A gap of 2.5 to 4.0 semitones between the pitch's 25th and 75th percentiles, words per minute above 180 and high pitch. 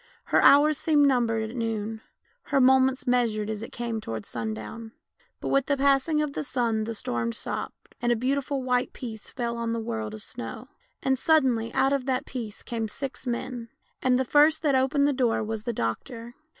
Yes: average, 3.3 semitones; average, 195 wpm; high, 245 Hz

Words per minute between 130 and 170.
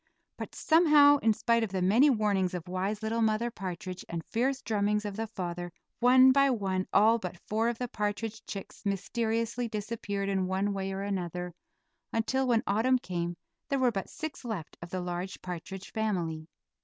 No: average, 180 wpm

